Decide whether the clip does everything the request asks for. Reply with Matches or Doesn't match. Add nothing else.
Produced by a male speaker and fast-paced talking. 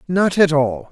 Doesn't match